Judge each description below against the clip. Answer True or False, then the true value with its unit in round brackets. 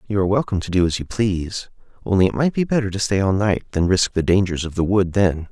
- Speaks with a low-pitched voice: True (100 Hz)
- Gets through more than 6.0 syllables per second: True (6.4 syllables/s)